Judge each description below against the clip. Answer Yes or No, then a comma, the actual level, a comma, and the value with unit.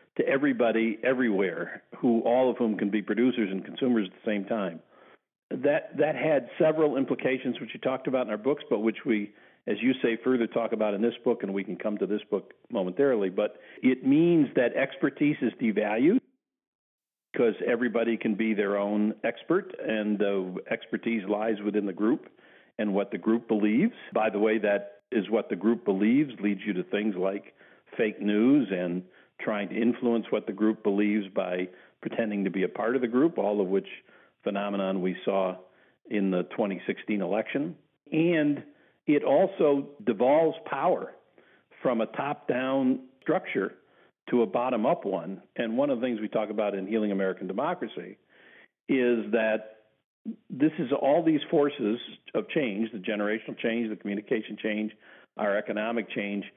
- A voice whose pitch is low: Yes, low, 110 Hz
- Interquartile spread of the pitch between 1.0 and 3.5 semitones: No, average, 3.9 semitones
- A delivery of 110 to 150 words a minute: No, average, 170 wpm